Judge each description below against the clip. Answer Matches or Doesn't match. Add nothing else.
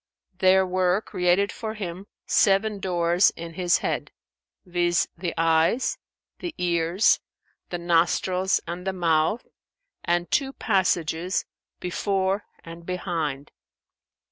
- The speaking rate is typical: Doesn't match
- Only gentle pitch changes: Matches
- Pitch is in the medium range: Matches